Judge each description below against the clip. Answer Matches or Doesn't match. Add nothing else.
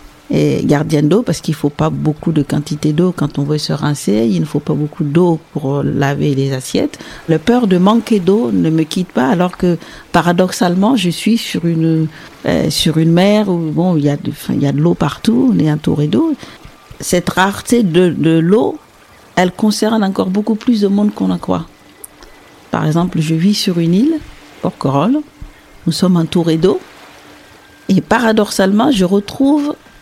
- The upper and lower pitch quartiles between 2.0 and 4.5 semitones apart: Doesn't match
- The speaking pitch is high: Doesn't match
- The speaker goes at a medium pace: Matches